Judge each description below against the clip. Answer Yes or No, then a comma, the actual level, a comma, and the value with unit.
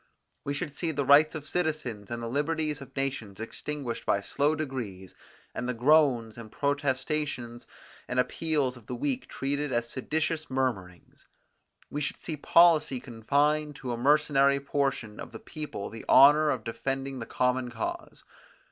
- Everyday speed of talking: Yes, average, 155 wpm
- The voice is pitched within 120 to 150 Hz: Yes, low, 135 Hz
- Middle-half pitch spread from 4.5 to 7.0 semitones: No, average, 3.8 semitones